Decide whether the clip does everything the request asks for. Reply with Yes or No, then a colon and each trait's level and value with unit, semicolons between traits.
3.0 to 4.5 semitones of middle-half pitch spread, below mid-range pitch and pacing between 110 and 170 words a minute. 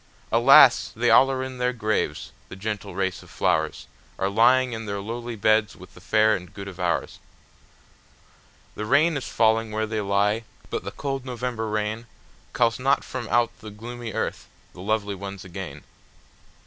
Yes: average, 3.3 semitones; low, 110 Hz; average, 160 wpm